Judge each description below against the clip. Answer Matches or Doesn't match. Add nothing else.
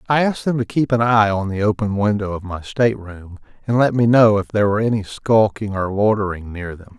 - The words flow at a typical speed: Doesn't match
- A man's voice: Matches